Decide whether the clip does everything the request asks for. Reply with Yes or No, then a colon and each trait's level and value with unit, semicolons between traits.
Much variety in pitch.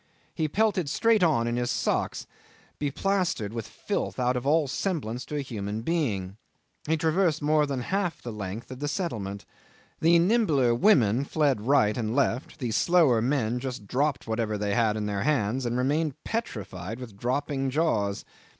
Yes: wide, 5.8 semitones